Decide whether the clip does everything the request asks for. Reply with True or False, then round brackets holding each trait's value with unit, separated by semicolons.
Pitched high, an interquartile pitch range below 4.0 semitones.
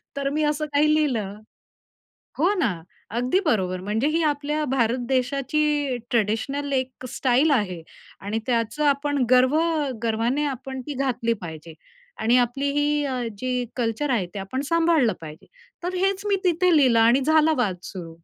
False (260 Hz; 4.6 semitones)